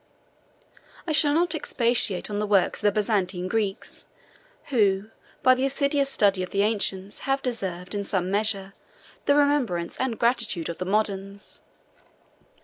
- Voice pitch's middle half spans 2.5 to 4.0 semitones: No, average, 4.9 semitones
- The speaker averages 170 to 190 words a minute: No, average, 145 wpm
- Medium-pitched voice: No, high, 210 Hz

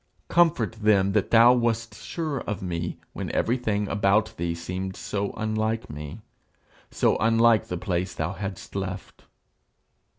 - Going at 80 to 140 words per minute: Yes, slow, 135 wpm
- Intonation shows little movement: No, average, 3.4 semitones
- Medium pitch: No, low, 105 Hz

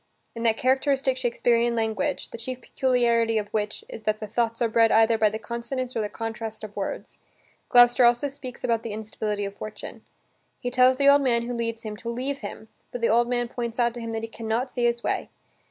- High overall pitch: Yes, high, 235 Hz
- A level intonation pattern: Yes, narrow, 1.8 semitones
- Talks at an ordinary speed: No, fast, 225 wpm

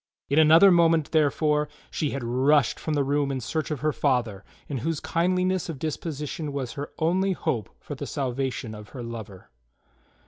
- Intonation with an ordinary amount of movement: Yes, average, 3.7 semitones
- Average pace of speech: Yes, average, 180 wpm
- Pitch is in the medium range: Yes, medium, 145 Hz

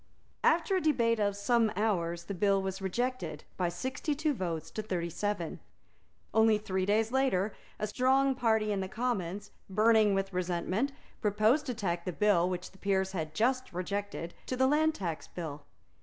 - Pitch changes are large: No, average, 4.8 semitones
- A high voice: Yes, high, 205 Hz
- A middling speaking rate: Yes, average, 170 wpm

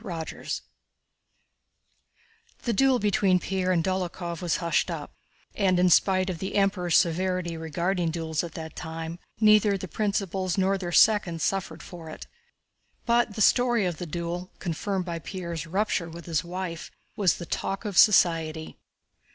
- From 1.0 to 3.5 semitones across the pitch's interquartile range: Yes, narrow, 2.6 semitones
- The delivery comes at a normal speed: Yes, average, 155 wpm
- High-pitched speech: No, medium, 180 Hz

